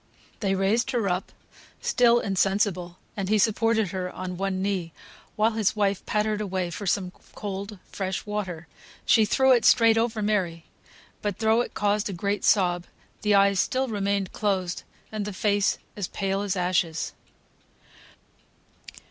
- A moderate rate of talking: Yes, average, 150 wpm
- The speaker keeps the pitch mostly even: Yes, narrow, 2.3 semitones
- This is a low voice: No, high, 200 Hz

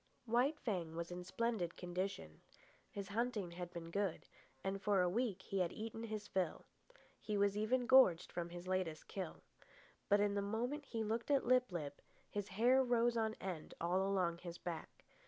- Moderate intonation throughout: Yes, average, 4.4 semitones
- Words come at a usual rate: Yes, average, 180 wpm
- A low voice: No, high, 200 Hz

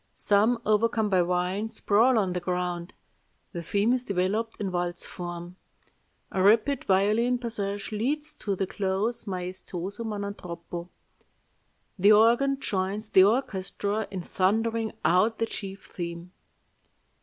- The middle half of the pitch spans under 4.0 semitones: Yes, average, 3.5 semitones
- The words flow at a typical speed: No, slow, 130 wpm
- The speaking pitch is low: No, high, 200 Hz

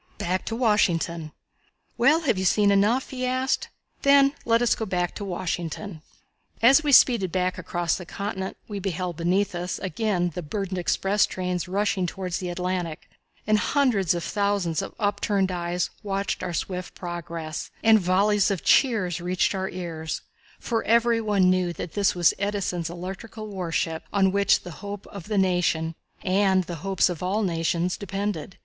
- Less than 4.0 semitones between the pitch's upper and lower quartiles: Yes, average, 2.8 semitones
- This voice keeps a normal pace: Yes, average, 170 wpm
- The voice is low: No, high, 190 Hz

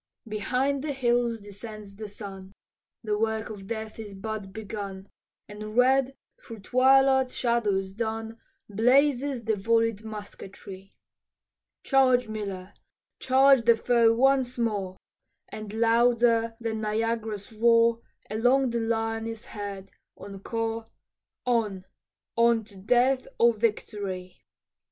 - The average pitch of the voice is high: Yes, high, 225 Hz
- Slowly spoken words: Yes, slow, 115 wpm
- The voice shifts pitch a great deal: No, narrow, 2.5 semitones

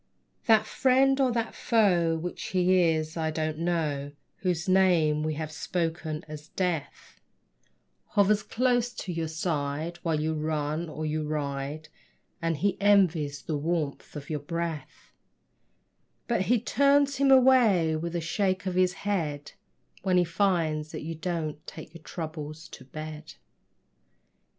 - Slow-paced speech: No, average, 145 wpm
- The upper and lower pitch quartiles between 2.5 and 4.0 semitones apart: Yes, average, 3.7 semitones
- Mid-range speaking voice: Yes, medium, 165 Hz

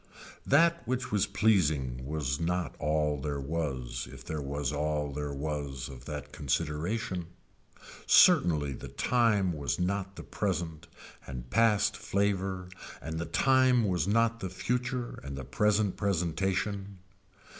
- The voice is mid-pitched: No, very low, 85 Hz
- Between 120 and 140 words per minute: Yes, slow, 135 wpm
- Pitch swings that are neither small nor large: No, wide, 5.7 semitones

